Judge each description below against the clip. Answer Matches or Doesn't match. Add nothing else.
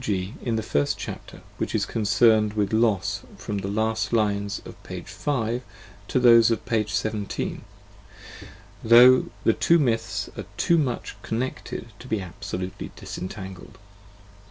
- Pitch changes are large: Doesn't match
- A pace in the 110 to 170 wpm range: Matches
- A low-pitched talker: Matches